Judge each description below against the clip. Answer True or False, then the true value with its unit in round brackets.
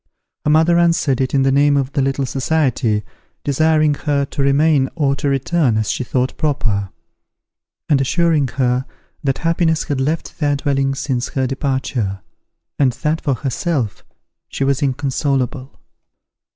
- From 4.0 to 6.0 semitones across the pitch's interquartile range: False (2.5 semitones)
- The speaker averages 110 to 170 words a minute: True (150 wpm)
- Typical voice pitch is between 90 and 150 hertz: True (140 Hz)